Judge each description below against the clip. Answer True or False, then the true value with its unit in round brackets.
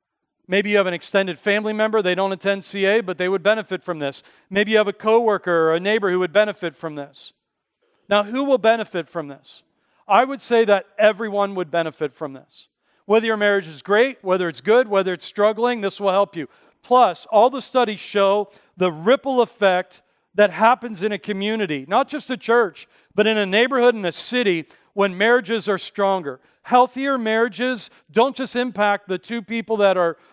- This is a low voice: False (205 Hz)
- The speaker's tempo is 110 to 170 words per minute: False (195 wpm)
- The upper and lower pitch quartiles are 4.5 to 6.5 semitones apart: False (3.8 semitones)